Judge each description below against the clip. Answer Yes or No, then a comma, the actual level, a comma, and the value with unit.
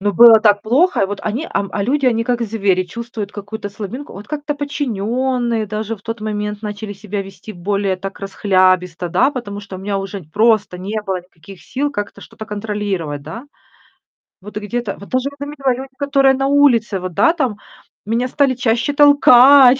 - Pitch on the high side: Yes, high, 215 Hz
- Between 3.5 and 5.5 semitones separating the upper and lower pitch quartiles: Yes, average, 4.4 semitones